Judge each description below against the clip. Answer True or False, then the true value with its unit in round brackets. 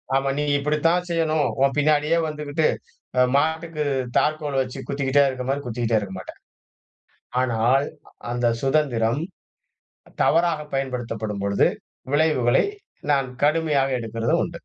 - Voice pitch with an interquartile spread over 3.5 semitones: True (4.0 semitones)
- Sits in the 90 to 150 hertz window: True (140 Hz)